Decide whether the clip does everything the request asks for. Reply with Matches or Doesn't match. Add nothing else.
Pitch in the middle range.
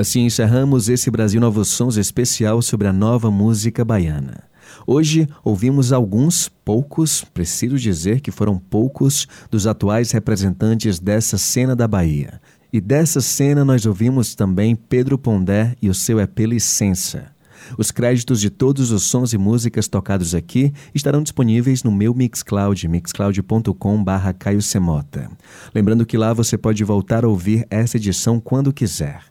Doesn't match